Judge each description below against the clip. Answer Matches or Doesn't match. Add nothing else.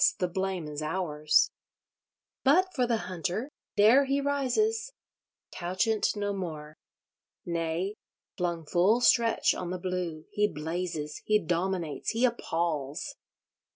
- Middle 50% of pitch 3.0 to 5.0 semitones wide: Doesn't match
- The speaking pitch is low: Doesn't match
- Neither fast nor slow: Doesn't match